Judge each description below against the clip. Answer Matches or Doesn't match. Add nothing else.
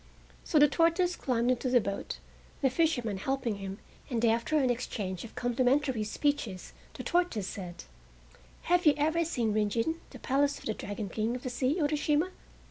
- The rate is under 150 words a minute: Doesn't match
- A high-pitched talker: Matches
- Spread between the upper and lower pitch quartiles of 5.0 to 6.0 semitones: Matches